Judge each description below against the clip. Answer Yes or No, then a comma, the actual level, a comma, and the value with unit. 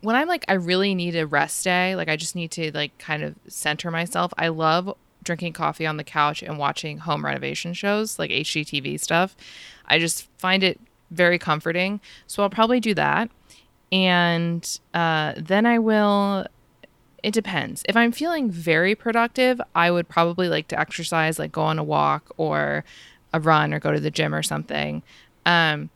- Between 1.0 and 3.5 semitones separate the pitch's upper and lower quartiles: No, average, 4.2 semitones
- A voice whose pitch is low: No, medium, 170 Hz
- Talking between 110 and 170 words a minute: No, average, 185 wpm